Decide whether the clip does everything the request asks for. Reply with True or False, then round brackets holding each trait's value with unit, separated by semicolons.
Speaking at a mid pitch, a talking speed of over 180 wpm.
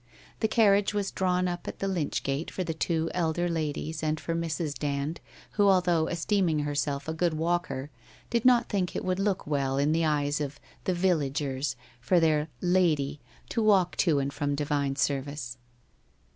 True (160 Hz; 200 wpm)